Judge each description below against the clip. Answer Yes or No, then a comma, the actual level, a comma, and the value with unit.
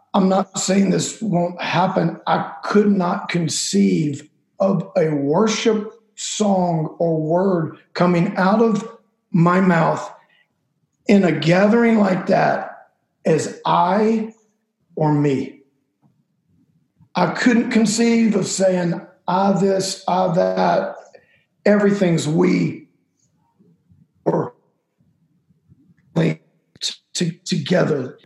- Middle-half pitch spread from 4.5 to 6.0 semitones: No, average, 3.5 semitones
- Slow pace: Yes, slow, 95 wpm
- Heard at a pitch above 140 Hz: Yes, high, 190 Hz